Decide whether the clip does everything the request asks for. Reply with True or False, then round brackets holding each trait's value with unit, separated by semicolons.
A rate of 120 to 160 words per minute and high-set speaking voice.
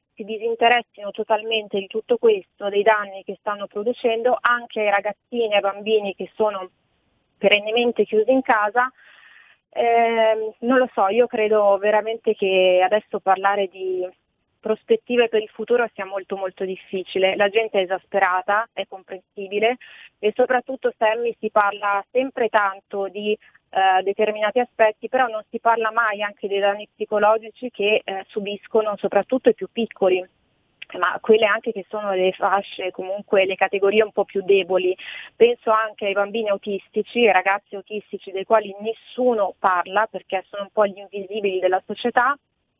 True (155 wpm; 210 Hz)